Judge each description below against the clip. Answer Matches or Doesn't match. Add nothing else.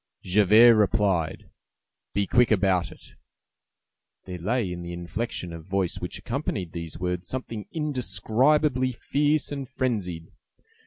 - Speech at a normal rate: Doesn't match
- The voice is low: Matches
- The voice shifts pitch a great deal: Matches